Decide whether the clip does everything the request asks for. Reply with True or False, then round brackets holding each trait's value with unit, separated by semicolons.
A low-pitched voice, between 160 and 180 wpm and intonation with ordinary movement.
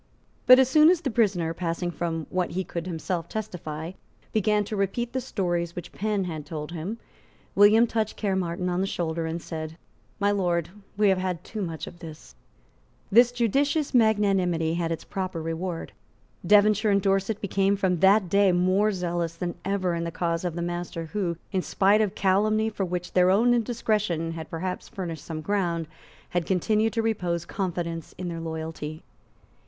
False (185 Hz; 175 wpm; 3.7 semitones)